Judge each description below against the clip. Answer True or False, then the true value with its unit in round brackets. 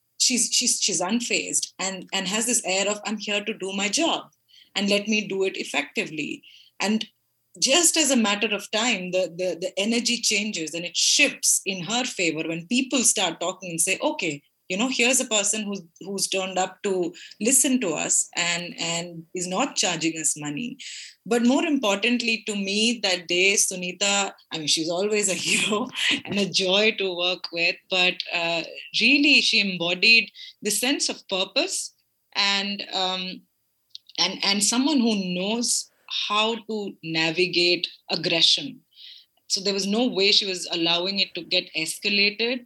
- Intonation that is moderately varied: True (4.1 semitones)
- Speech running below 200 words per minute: True (165 wpm)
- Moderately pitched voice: False (200 Hz)